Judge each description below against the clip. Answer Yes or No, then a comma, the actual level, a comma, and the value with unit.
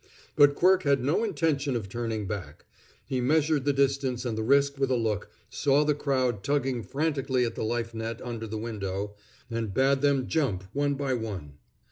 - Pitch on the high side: No, low, 130 Hz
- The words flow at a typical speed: Yes, average, 185 wpm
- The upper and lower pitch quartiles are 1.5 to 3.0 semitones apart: No, average, 4.1 semitones